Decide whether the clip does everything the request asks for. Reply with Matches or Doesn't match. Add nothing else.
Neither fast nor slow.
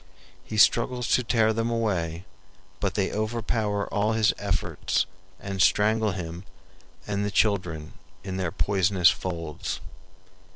Doesn't match